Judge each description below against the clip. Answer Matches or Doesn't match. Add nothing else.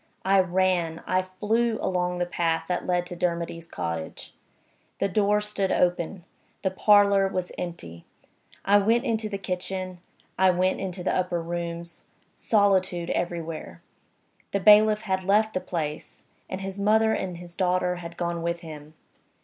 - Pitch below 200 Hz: Matches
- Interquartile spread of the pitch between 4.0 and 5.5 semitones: Doesn't match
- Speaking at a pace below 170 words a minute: Matches